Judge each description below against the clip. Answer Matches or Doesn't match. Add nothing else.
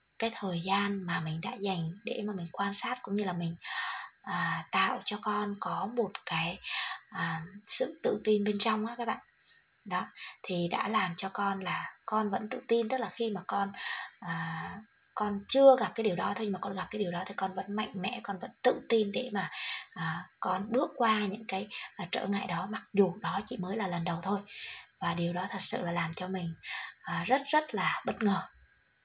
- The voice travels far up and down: Doesn't match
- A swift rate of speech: Doesn't match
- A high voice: Matches